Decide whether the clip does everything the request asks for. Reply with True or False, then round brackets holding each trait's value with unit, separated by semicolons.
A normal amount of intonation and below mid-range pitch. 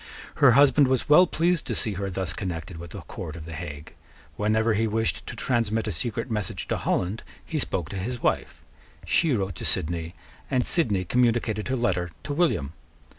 False (6.0 semitones; 110 Hz)